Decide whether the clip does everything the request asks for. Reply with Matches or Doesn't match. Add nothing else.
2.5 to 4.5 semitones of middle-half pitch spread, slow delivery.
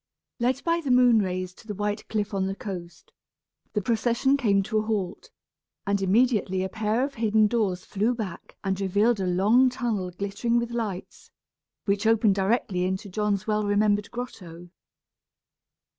Doesn't match